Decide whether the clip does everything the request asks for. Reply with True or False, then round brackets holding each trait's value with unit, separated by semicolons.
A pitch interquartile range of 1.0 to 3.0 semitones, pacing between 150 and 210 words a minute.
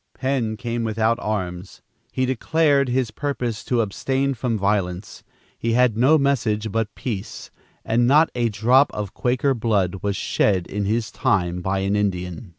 False (3.9 semitones; 155 wpm)